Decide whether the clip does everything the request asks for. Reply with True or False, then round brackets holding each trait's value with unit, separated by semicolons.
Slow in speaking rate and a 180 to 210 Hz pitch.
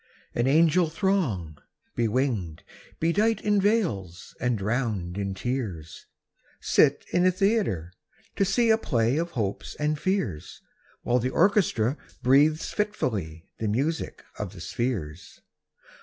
False (125 wpm; 125 Hz)